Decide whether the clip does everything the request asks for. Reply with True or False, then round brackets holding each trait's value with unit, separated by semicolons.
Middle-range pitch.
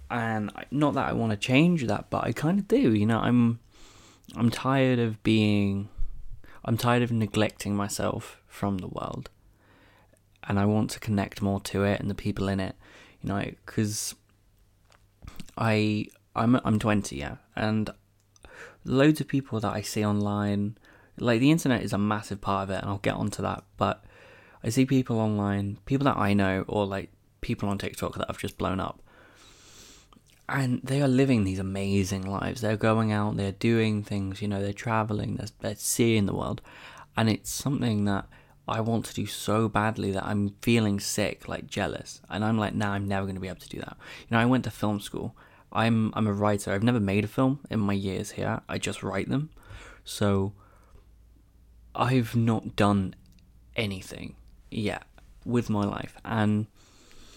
False (105 Hz)